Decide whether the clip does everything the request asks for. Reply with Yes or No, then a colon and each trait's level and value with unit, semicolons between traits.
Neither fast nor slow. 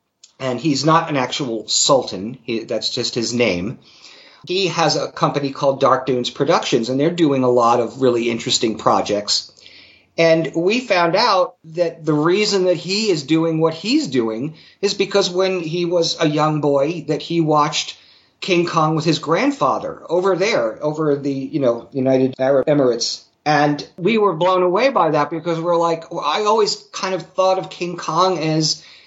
Yes: average, 180 wpm